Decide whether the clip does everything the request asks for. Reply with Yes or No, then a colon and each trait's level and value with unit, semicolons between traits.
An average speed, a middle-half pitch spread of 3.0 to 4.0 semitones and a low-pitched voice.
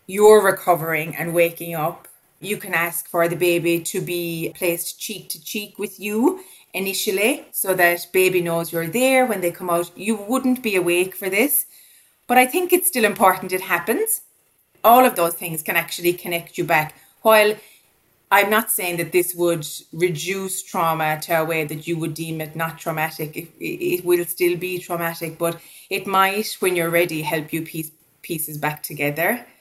No: average, 180 wpm; average, 3.7 semitones; medium, 175 Hz